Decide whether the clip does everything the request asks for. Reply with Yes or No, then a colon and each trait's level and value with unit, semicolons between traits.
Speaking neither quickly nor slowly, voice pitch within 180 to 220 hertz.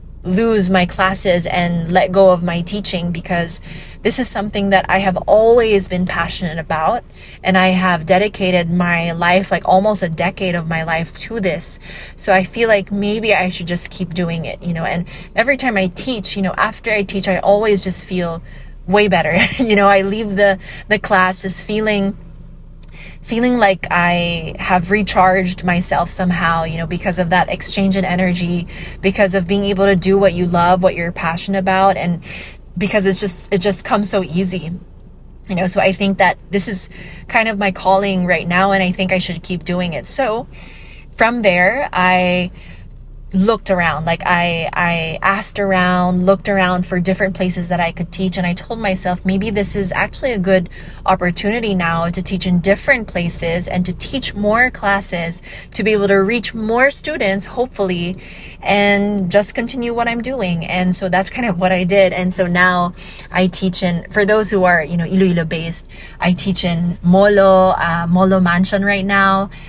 Yes: average, 190 wpm; medium, 185 Hz